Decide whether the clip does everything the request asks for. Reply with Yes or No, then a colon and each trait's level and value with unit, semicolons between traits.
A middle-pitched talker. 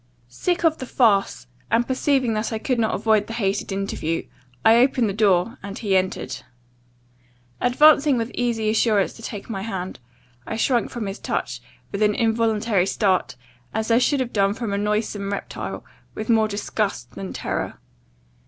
No: high, 220 Hz